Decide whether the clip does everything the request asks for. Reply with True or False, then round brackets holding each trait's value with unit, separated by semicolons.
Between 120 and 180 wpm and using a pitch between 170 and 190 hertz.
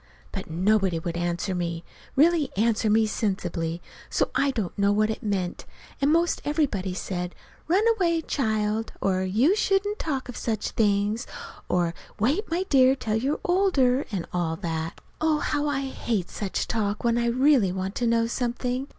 False (165 wpm; 225 Hz)